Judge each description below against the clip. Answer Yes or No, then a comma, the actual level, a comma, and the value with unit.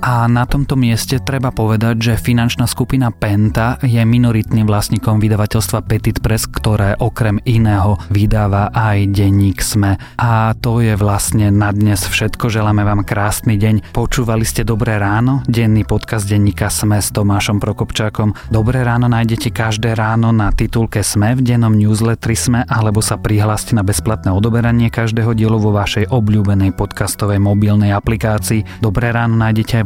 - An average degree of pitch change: No, narrow, 2.0 semitones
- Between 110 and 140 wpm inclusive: No, average, 150 wpm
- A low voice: Yes, low, 110 Hz